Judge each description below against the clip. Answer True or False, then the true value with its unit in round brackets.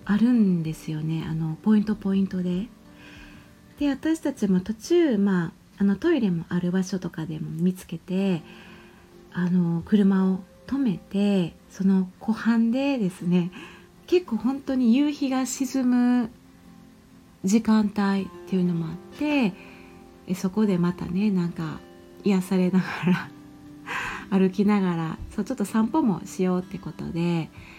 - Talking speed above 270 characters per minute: False (260 characters per minute)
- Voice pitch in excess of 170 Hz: True (190 Hz)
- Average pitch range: True (3.9 semitones)